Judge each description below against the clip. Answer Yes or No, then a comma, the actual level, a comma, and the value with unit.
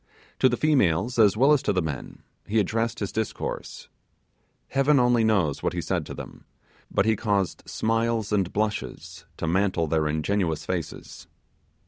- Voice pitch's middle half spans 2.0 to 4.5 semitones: No, average, 4.9 semitones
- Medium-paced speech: Yes, average, 160 wpm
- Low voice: Yes, low, 105 Hz